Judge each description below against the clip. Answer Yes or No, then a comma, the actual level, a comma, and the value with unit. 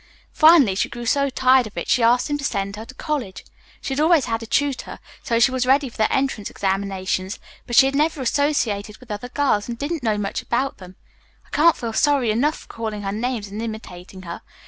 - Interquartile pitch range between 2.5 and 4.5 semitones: No, average, 5.1 semitones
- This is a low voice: No, high, 235 Hz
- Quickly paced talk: Yes, fast, 225 wpm